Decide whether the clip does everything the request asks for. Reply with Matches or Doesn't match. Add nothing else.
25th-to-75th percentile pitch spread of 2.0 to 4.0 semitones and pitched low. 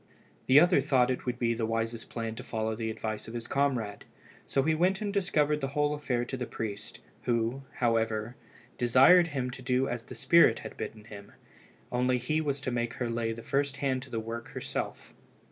Matches